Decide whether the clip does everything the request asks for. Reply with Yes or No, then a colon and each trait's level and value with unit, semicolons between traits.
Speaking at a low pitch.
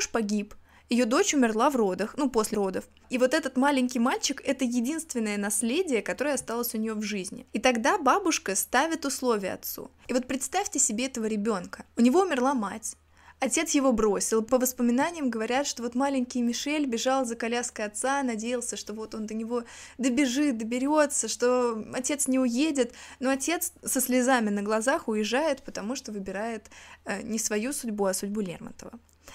No: high, 245 Hz